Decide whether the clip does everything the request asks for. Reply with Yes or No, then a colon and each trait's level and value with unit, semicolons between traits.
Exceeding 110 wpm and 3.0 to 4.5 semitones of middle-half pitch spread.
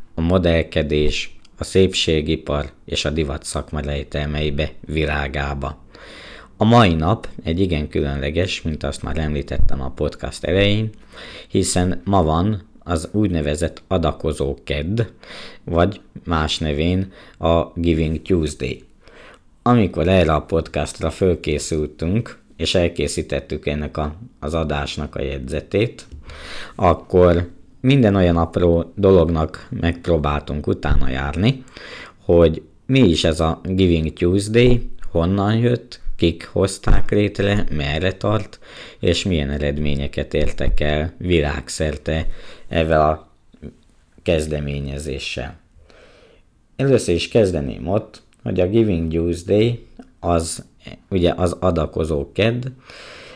No: slow, 105 wpm; average, 3.9 semitones